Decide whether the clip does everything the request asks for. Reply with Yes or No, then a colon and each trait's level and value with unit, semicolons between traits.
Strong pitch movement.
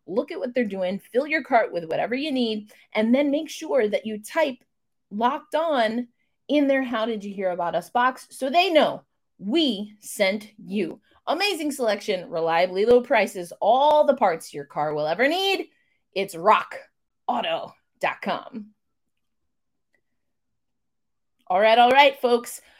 Yes: wide, 5.7 semitones